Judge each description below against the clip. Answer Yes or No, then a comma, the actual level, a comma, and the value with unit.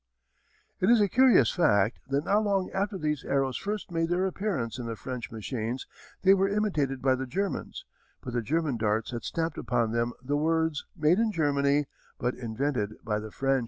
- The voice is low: No, medium, 145 Hz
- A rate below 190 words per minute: No, average, 195 wpm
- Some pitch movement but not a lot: No, wide, 7.4 semitones